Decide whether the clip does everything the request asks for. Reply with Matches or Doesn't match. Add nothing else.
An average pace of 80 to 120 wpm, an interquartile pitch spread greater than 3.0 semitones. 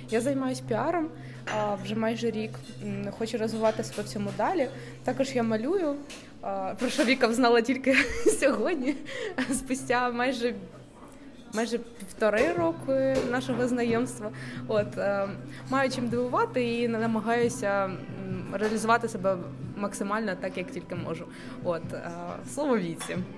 Matches